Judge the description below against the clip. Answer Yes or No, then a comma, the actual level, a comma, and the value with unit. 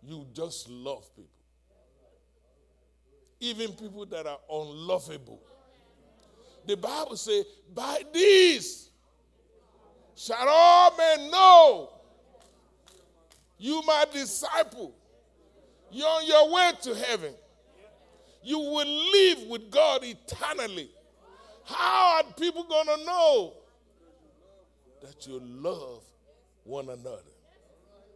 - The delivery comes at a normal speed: No, slow, 95 wpm